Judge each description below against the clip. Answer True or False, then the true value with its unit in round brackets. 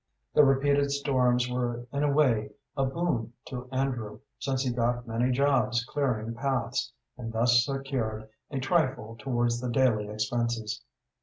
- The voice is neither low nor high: False (125 Hz)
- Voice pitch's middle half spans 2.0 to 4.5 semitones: True (2.6 semitones)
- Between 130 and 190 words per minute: True (145 wpm)